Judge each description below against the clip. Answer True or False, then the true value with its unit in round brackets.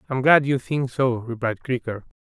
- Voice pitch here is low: True (125 Hz)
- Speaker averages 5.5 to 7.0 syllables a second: False (4.8 syllables/s)